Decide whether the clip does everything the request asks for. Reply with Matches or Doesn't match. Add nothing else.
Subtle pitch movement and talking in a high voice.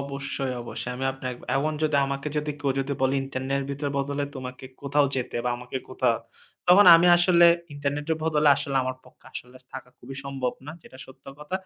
Doesn't match